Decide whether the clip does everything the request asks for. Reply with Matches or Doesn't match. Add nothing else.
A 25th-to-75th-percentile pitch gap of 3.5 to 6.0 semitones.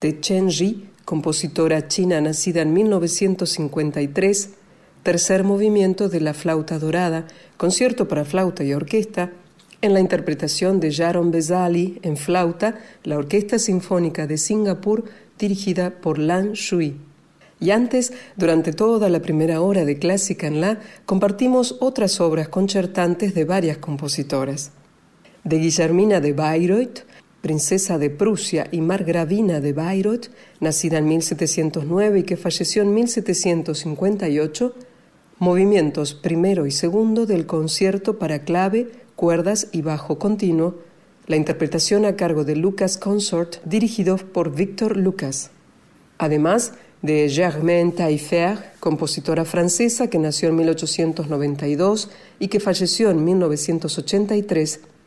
Matches